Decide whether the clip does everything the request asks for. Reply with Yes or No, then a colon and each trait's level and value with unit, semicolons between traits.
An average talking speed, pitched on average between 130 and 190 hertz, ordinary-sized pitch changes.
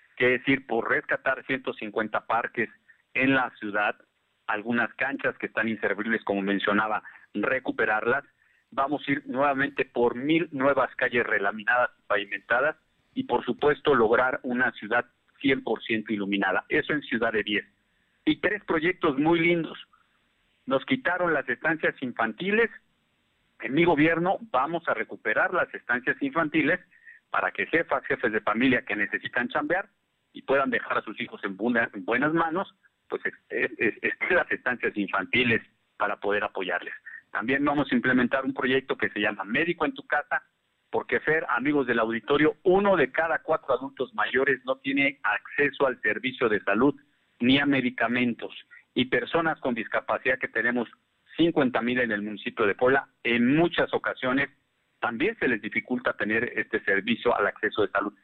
No: average, 155 wpm; medium, 140 Hz; wide, 7.4 semitones